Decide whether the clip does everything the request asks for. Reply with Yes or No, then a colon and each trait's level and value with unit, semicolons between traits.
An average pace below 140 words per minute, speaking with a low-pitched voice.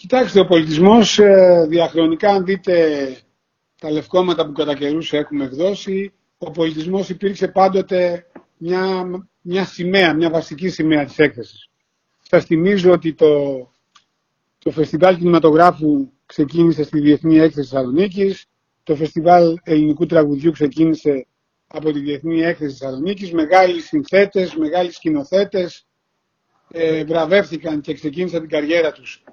No: average, 120 wpm; medium, 165 Hz